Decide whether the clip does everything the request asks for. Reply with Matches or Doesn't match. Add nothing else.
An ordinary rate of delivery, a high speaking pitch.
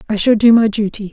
Doesn't match